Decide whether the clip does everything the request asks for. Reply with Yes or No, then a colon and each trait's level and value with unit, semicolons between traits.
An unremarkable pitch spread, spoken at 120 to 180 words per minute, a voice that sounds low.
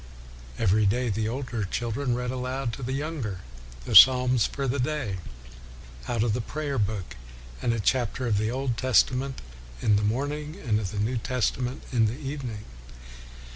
Yes: average, 3.5 semitones; average, 170 wpm; low, 125 Hz